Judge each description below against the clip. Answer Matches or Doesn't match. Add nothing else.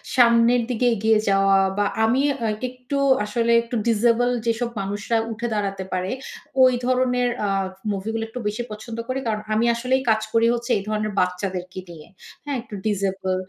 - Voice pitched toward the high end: Matches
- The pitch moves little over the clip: Doesn't match